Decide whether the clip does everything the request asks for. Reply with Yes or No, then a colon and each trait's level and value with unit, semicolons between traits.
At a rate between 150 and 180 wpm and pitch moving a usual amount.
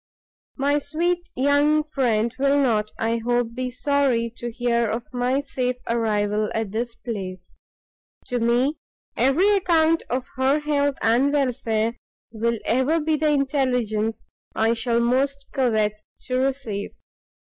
No: slow, 135 wpm; average, 3.6 semitones